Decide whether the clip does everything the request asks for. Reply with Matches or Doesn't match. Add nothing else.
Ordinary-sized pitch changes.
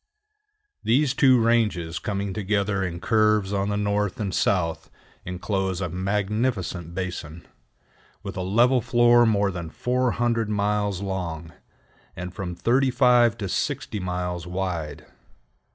Matches